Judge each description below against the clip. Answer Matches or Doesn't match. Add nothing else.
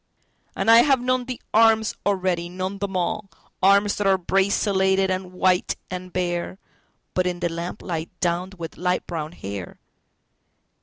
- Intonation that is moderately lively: Doesn't match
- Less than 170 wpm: Matches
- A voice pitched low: Doesn't match